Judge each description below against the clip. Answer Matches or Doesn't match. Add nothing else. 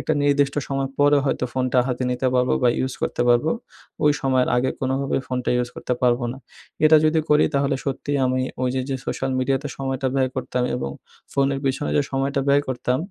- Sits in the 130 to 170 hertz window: Matches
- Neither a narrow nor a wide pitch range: Doesn't match